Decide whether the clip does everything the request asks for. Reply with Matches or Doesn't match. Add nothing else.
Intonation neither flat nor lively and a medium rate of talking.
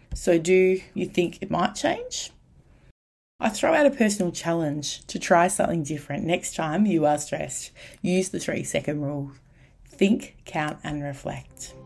Matches